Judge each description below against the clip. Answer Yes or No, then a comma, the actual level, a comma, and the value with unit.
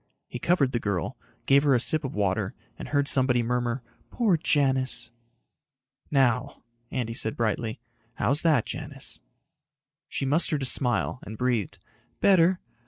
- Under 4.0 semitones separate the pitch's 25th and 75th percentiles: Yes, average, 3.5 semitones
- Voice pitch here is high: No, low, 130 Hz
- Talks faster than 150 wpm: No, average, 140 wpm